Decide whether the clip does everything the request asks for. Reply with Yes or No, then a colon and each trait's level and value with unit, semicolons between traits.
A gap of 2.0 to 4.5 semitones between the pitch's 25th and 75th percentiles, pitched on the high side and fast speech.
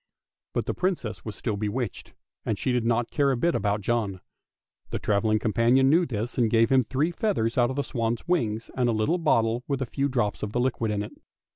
No: average, 3.5 semitones; low, 120 Hz; fast, 220 wpm